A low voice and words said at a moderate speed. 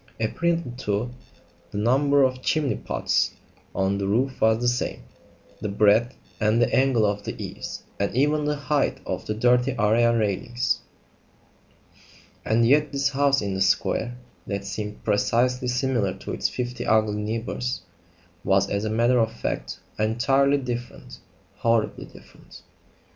Yes: low, 120 Hz; average, 145 wpm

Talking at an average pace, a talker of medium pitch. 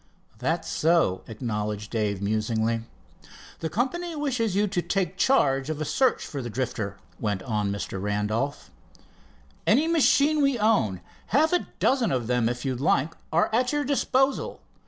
Yes: average, 155 wpm; medium, 145 Hz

